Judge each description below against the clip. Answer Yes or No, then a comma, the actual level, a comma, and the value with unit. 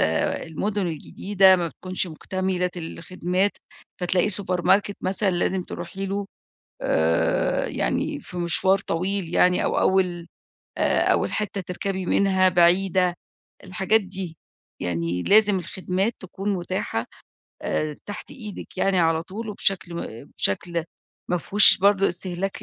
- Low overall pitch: No, medium, 185 Hz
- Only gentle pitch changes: Yes, narrow, 2.1 semitones